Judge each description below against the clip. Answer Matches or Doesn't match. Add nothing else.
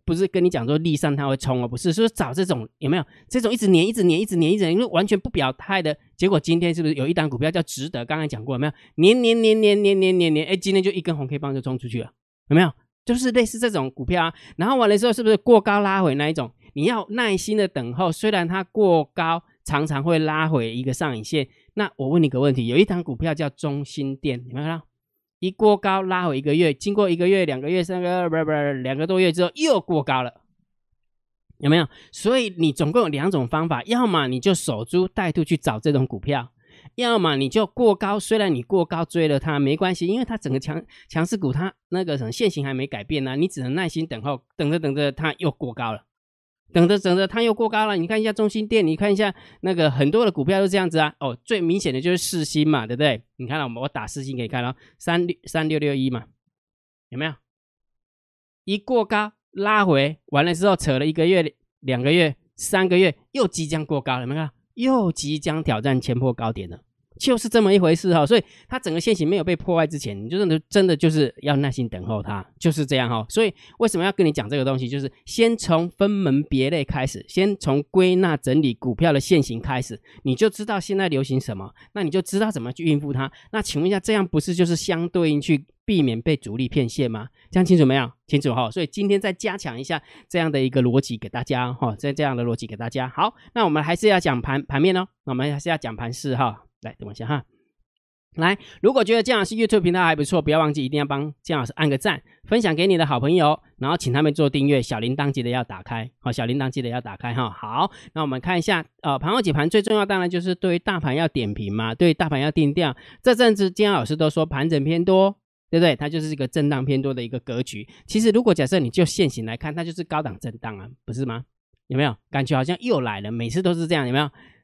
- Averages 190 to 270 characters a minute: Doesn't match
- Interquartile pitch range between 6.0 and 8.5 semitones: Doesn't match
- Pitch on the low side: Doesn't match